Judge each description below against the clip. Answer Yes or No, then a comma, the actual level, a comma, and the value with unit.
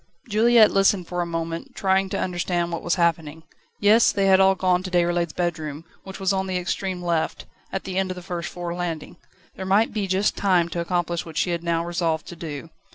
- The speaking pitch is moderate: Yes, medium, 175 Hz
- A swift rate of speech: Yes, fast, 220 wpm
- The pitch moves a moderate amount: No, narrow, 2.1 semitones